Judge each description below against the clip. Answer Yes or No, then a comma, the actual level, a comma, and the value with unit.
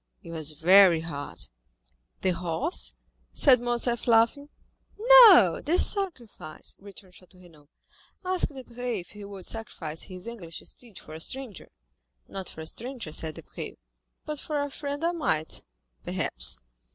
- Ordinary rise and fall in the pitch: No, wide, 8.3 semitones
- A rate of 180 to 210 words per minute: No, average, 140 wpm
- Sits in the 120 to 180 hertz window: No, high, 210 Hz